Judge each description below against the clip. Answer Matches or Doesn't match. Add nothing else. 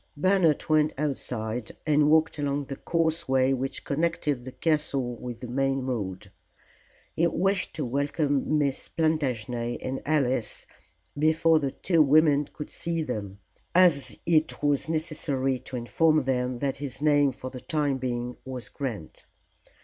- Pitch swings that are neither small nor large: Matches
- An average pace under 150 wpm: Matches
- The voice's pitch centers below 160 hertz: Matches